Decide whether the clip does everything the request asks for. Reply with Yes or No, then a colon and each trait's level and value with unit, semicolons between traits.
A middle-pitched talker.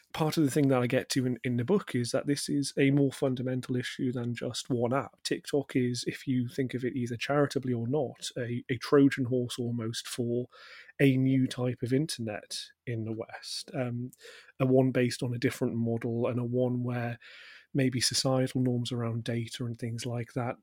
No: low, 125 Hz